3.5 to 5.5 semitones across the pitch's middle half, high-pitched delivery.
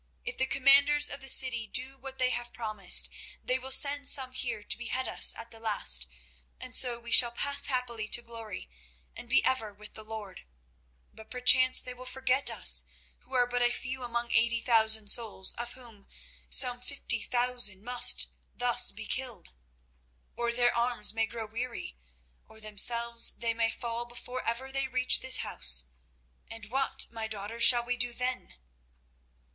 No: narrow, 2.4 semitones; high, 240 Hz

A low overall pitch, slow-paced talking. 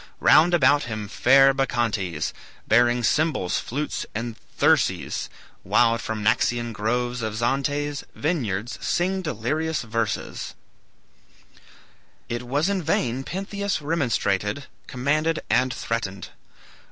Yes: low, 125 Hz; slow, 105 wpm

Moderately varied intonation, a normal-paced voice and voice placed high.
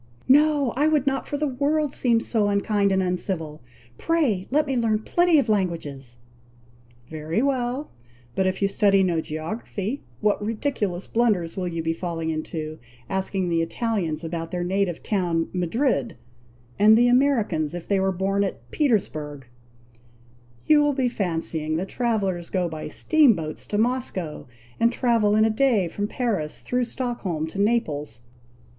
No: wide, 6.5 semitones; average, 155 wpm; high, 200 Hz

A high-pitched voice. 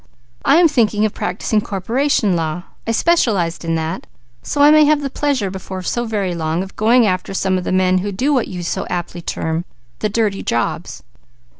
Yes: high, 195 Hz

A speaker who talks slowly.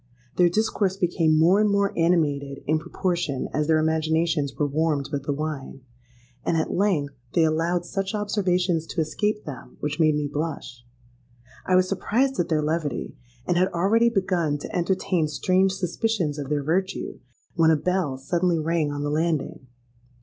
No: average, 165 wpm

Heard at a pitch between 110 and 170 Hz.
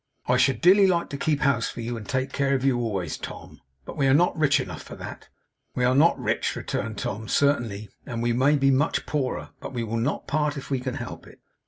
Yes: low, 135 Hz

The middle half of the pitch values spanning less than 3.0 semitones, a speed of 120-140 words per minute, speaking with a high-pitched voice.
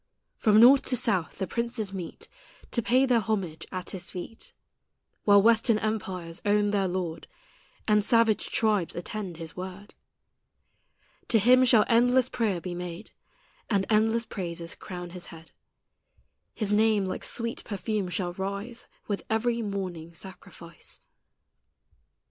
No: average, 3.8 semitones; slow, 135 wpm; high, 205 Hz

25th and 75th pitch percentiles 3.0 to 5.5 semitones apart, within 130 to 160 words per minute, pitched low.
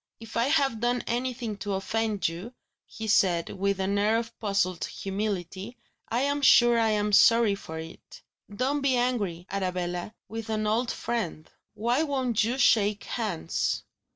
No: average, 3.4 semitones; average, 155 wpm; high, 220 Hz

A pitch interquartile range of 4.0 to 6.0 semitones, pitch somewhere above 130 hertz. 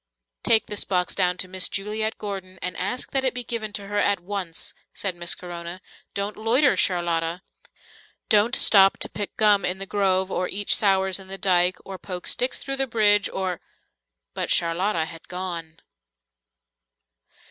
No: narrow, 2.6 semitones; high, 190 Hz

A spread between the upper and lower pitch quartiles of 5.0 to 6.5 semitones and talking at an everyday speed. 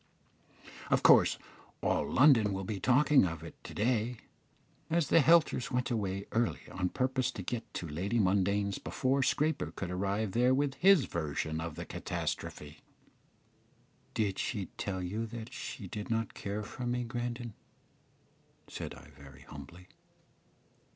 Yes: average, 5.3 semitones; average, 145 wpm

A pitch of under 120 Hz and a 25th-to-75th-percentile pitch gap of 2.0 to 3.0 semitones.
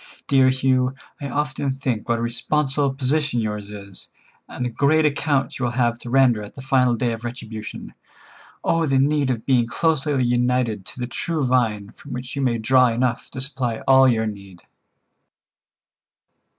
No: low, 125 Hz; narrow, 2.6 semitones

